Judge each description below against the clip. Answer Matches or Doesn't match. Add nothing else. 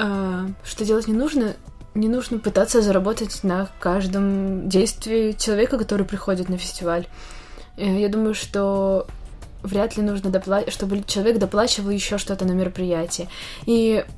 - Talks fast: Doesn't match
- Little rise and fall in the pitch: Matches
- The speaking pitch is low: Doesn't match